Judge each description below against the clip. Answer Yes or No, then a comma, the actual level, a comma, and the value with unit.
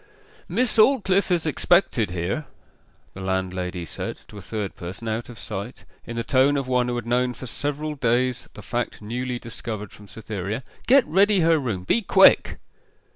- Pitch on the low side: Yes, low, 120 Hz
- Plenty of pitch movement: Yes, wide, 6.3 semitones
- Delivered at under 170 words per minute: No, average, 175 wpm